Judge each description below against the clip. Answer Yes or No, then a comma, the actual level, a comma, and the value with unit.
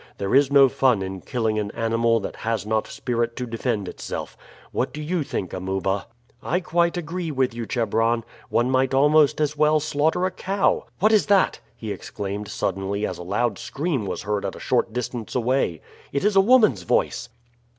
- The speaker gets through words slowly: No, average, 190 wpm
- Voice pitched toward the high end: No, low, 120 Hz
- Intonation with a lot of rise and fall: Yes, wide, 6.2 semitones